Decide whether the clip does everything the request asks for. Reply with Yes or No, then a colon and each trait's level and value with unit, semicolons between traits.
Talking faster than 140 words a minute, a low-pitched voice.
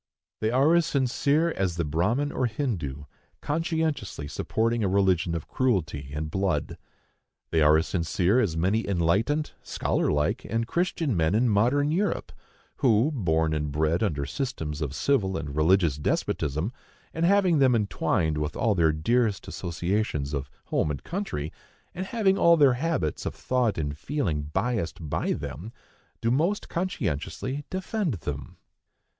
Yes: average, 150 wpm; low, 100 Hz